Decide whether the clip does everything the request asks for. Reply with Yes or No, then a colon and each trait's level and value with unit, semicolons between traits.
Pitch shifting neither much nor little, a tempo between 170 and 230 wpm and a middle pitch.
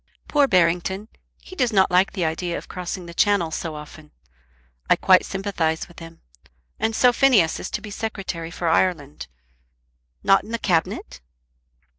No: average, 3.8 semitones; average, 160 wpm; medium, 180 Hz